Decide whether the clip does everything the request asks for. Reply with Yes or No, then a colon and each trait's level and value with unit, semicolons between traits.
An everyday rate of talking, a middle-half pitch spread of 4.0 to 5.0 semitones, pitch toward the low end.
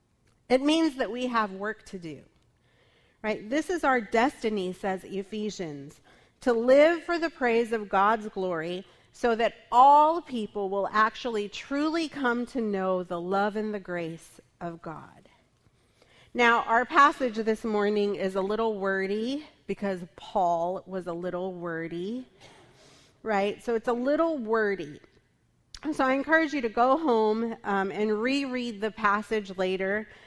No: average, 145 wpm; average, 4.5 semitones; high, 220 Hz